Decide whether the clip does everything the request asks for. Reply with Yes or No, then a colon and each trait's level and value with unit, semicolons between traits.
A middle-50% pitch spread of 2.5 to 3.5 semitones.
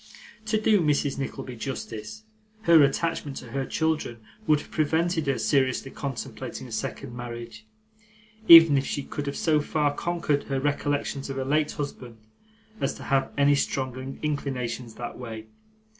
Yes: average, 2.8 semitones